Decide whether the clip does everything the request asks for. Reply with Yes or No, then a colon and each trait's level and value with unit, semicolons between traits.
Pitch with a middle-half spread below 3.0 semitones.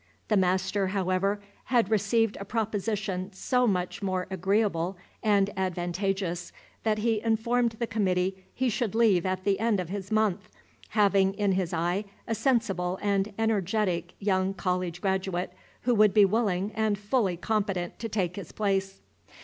Yes: narrow, 2.6 semitones